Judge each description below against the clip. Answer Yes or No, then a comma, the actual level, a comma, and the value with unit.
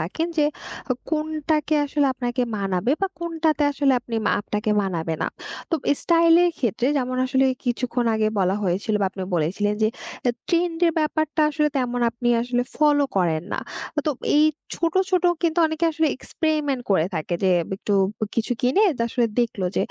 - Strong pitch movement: Yes, wide, 6.8 semitones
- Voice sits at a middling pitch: No, very high, 255 Hz